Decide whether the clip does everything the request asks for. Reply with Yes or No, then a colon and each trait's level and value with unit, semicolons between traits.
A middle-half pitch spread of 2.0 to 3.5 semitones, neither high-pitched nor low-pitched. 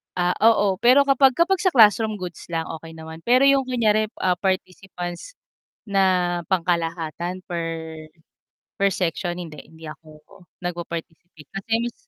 No: average, 4.5 semitones; medium, 180 Hz